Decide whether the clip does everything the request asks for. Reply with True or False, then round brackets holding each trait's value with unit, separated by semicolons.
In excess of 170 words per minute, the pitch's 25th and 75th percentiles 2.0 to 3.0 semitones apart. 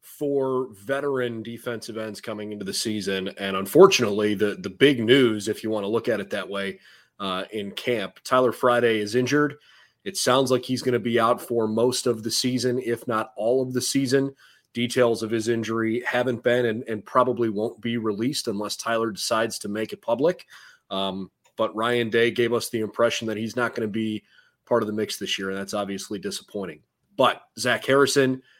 True (200 wpm; 2.6 semitones)